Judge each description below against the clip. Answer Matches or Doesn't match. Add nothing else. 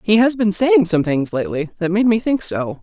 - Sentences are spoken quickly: Matches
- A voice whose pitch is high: Matches